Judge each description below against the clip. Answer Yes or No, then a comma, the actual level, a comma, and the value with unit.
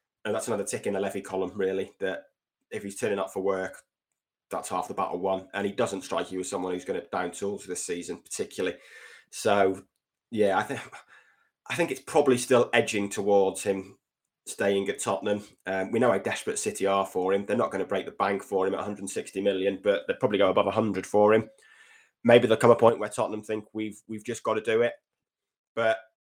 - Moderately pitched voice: No, low, 100 Hz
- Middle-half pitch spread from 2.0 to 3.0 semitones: Yes, narrow, 2.4 semitones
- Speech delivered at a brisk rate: Yes, fast, 220 wpm